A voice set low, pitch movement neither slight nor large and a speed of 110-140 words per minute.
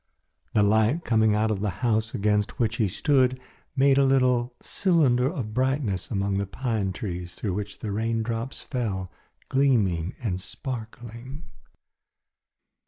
Yes: low, 115 Hz; average, 4.0 semitones; slow, 135 wpm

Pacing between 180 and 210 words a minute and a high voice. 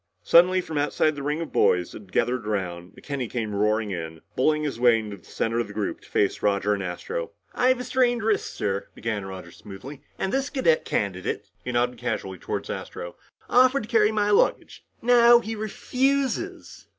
No: average, 195 wpm; low, 125 Hz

